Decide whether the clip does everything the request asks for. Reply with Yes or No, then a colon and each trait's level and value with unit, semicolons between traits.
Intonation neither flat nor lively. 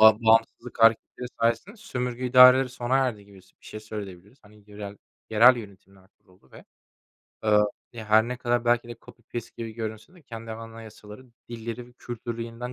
No: narrow, 2.3 semitones